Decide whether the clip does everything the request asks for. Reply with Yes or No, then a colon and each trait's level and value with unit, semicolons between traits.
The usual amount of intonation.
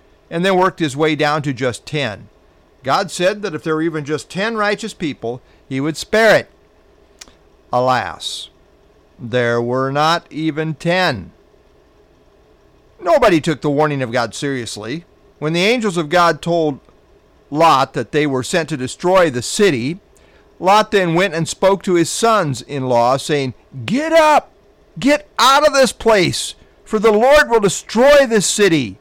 No: wide, 6.8 semitones